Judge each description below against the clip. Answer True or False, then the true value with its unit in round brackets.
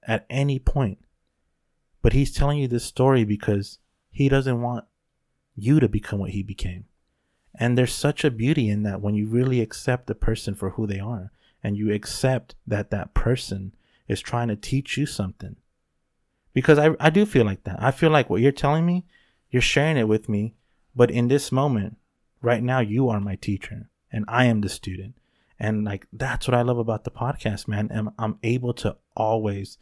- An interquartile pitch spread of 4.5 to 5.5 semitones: False (4.1 semitones)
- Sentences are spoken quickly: False (195 wpm)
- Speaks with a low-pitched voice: True (115 Hz)